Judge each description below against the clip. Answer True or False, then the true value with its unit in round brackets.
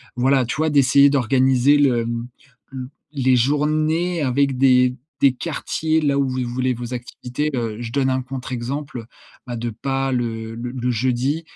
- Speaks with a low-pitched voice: True (130 Hz)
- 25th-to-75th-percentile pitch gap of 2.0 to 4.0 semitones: True (2.5 semitones)